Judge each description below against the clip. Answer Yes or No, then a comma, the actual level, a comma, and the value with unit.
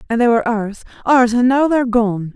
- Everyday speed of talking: No, fast, 255 wpm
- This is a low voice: No, high, 235 Hz